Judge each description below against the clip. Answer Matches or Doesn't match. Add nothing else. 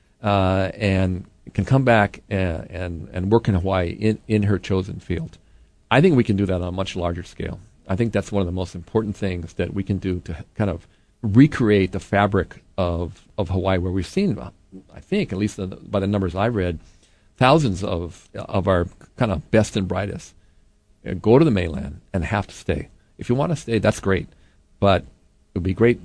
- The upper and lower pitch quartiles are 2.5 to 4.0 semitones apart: Matches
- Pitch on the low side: Matches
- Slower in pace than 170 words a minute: Doesn't match